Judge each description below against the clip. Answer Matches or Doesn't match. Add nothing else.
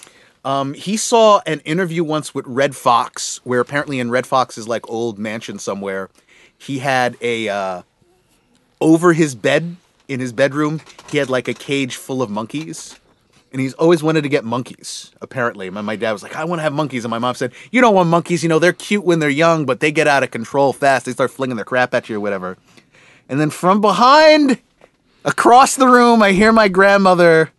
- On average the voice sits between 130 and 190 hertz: Matches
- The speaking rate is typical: Doesn't match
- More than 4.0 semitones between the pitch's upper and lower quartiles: Matches